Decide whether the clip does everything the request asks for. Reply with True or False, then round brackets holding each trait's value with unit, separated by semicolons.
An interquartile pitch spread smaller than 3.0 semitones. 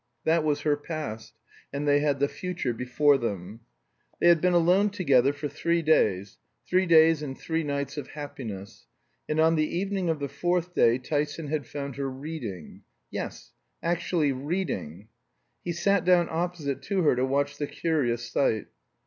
False (4.1 semitones)